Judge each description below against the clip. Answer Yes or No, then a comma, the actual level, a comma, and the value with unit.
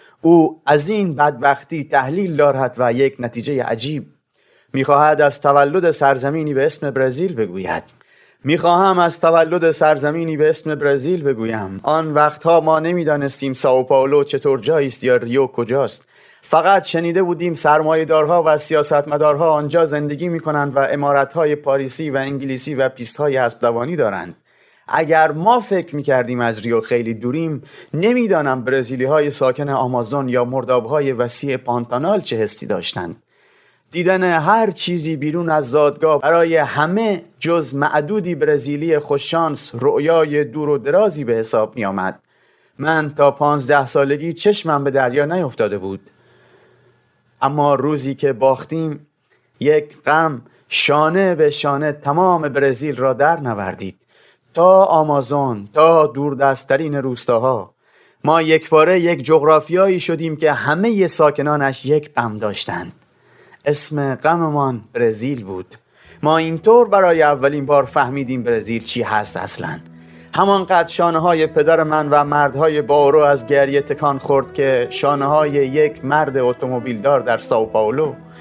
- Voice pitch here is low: No, medium, 145 Hz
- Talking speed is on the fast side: No, average, 135 wpm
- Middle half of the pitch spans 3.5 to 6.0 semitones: No, average, 3.0 semitones